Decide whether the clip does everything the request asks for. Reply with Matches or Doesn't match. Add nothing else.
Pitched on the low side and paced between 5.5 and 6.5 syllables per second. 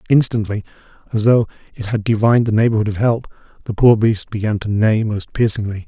Matches